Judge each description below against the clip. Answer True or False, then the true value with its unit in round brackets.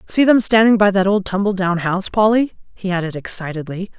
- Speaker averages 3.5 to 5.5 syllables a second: False (5.9 syllables/s)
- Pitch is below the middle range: False (195 Hz)